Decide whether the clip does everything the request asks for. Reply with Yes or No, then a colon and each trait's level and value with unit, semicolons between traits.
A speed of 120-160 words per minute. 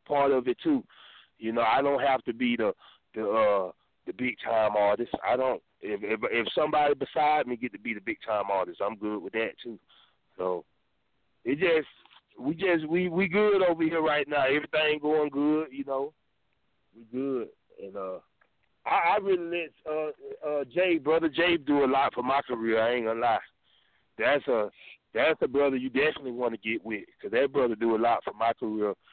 No: average, 200 wpm